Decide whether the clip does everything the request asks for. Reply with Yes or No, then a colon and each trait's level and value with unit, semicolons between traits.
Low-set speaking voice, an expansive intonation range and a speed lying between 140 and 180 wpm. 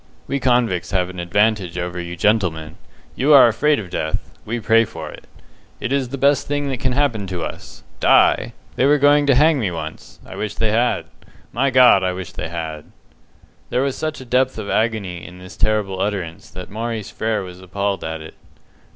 No: low, 105 Hz; wide, 6.0 semitones; average, 200 wpm